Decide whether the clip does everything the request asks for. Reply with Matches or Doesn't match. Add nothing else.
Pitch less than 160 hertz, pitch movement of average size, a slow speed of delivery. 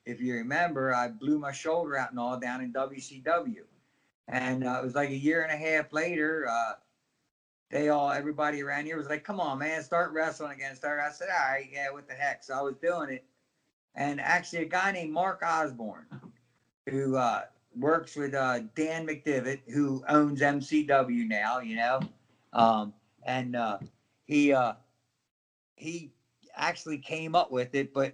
Doesn't match